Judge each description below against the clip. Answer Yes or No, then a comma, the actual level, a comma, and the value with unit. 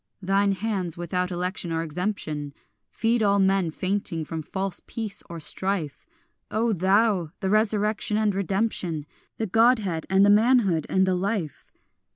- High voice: Yes, high, 195 Hz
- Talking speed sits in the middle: Yes, average, 145 wpm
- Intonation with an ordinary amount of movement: Yes, average, 3.5 semitones